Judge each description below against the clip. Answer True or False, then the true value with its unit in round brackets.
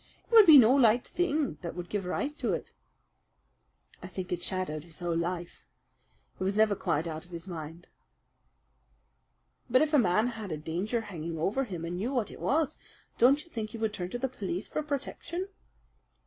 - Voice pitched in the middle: False (205 Hz)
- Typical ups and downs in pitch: False (6.8 semitones)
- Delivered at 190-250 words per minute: True (195 wpm)